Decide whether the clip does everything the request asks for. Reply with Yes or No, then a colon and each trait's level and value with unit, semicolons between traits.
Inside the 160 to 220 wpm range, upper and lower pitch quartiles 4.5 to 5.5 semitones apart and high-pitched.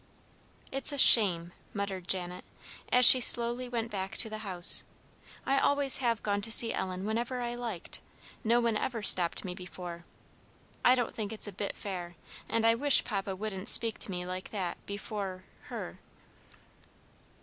No: average, 165 wpm; average, 4.1 semitones; high, 210 Hz